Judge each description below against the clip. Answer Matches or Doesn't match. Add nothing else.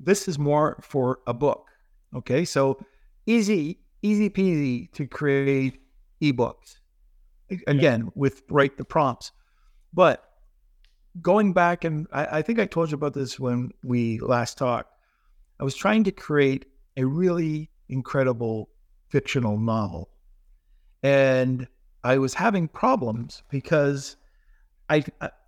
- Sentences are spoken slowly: Matches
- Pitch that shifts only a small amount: Doesn't match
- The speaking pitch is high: Doesn't match